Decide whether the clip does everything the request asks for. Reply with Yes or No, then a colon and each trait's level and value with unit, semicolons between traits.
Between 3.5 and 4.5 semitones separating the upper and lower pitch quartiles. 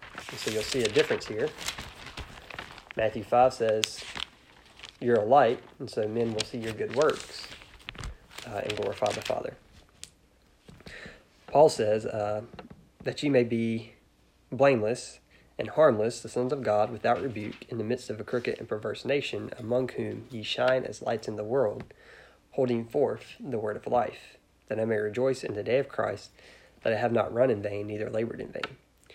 No: average, 3.1 semitones